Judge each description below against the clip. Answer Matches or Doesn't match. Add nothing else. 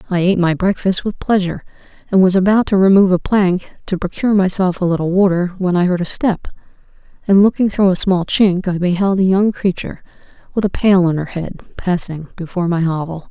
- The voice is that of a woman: Matches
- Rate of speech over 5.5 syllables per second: Matches